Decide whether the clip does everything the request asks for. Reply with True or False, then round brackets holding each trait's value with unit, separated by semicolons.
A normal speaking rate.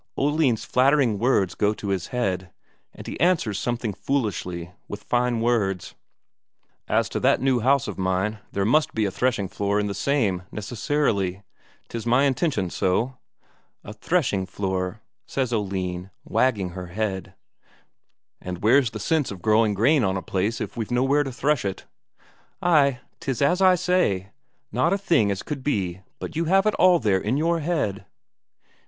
True (165 wpm)